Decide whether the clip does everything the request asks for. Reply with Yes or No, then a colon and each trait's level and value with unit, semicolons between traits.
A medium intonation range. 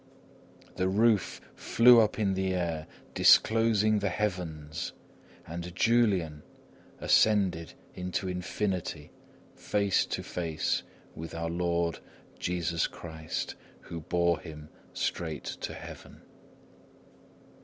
Yes: average, 3.6 semitones